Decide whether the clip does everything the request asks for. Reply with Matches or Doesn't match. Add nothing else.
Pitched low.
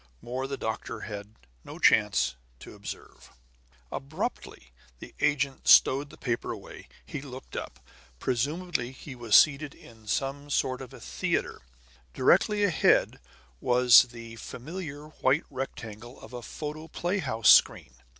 Matches